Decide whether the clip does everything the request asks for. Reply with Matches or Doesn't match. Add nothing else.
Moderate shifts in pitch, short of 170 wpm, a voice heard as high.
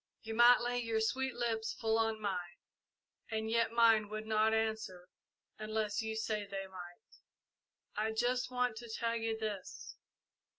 Doesn't match